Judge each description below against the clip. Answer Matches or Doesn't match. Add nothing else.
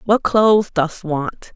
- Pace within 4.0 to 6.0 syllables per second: Doesn't match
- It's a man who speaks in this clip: Doesn't match